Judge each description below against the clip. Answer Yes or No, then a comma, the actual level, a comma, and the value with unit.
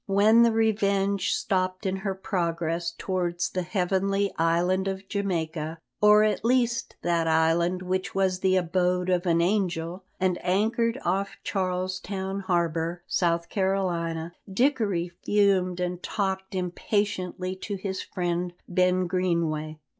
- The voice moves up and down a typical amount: No, narrow, 2.2 semitones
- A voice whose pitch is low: No, medium, 185 Hz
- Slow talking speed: Yes, slow, 130 wpm